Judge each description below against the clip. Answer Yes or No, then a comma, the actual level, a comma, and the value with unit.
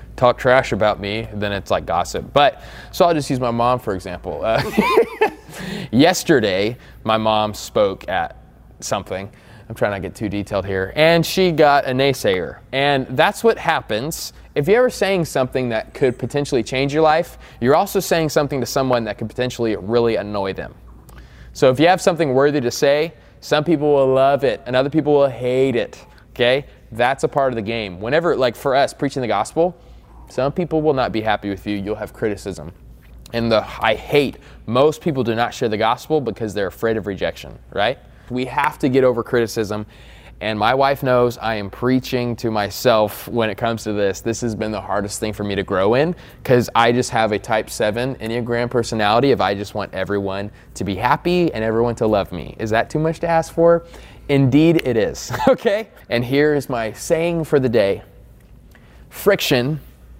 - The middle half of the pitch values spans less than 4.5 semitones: No, average, 5.2 semitones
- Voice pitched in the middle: No, low, 120 Hz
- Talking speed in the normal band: Yes, average, 195 wpm